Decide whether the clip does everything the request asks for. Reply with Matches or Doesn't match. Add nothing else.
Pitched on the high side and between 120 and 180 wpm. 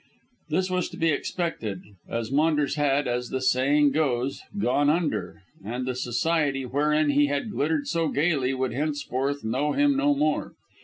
Doesn't match